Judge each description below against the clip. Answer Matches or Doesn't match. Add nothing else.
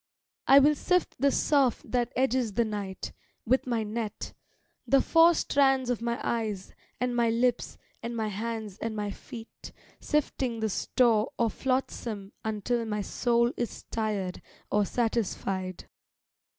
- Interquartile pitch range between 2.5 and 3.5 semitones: Matches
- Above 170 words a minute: Doesn't match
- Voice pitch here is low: Doesn't match